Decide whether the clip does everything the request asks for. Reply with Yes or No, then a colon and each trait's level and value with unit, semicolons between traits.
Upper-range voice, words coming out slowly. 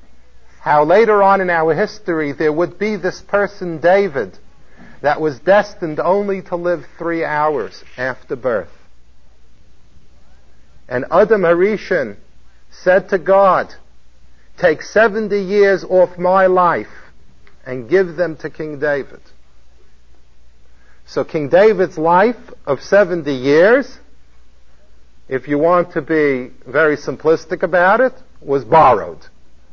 No: medium, 160 Hz; slow, 115 wpm